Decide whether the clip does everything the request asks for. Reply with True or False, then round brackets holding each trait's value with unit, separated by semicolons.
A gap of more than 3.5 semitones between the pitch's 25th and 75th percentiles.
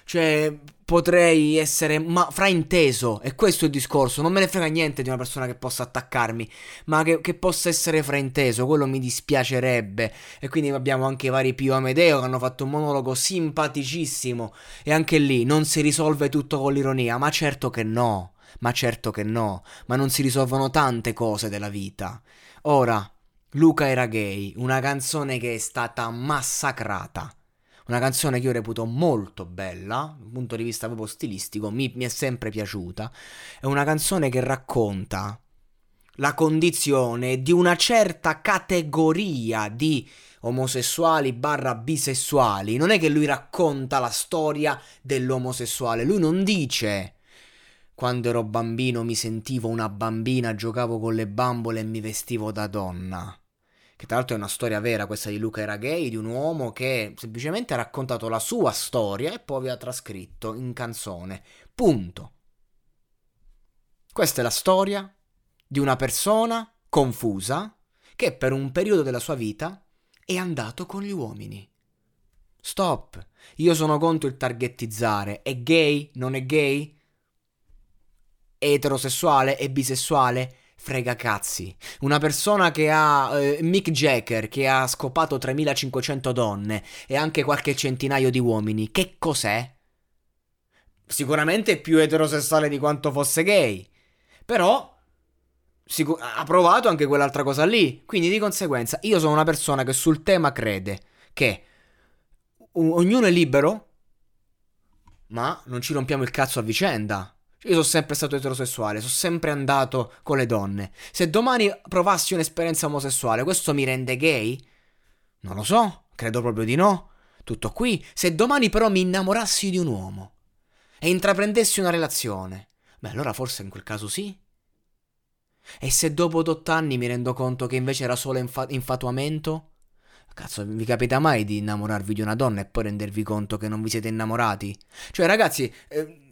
True (5.6 semitones)